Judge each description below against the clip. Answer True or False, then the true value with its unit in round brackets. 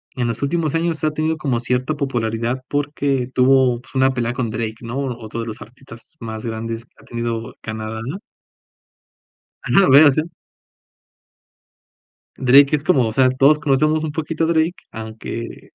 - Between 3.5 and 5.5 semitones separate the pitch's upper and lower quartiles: True (4.3 semitones)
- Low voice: True (130 Hz)